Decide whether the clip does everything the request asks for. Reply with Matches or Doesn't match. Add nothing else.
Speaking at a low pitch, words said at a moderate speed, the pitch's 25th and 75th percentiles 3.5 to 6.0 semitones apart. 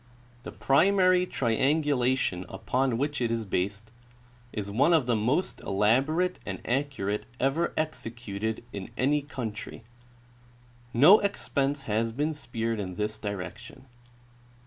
Doesn't match